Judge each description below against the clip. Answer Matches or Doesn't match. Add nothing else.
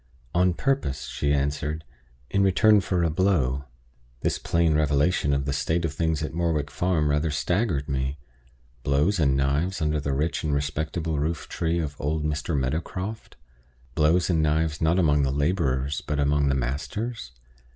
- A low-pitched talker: Matches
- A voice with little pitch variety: Doesn't match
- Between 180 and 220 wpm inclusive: Doesn't match